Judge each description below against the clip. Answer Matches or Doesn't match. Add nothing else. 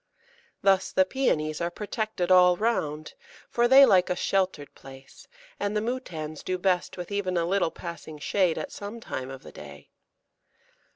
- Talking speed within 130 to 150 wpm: Doesn't match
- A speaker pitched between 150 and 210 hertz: Matches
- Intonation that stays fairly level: Doesn't match